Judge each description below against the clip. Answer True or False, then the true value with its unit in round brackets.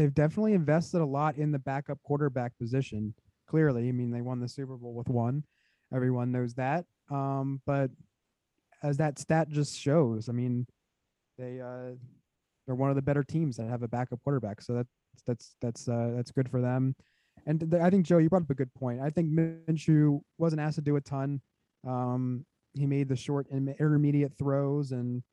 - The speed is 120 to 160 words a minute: False (195 wpm)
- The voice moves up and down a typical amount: True (3.1 semitones)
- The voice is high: False (135 Hz)